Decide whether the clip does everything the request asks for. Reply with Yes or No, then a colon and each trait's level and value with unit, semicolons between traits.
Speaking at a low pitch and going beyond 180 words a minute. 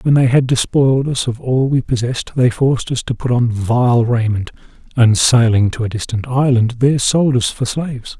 Yes: low, 120 Hz; fast, 205 wpm